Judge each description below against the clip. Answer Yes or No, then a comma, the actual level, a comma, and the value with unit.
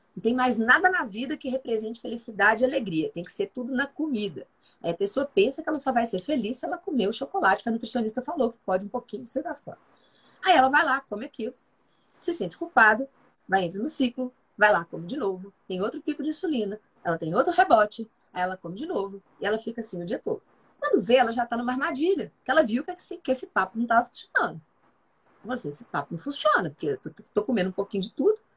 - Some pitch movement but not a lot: No, wide, 6.1 semitones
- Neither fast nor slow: No, fast, 245 wpm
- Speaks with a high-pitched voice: Yes, high, 245 Hz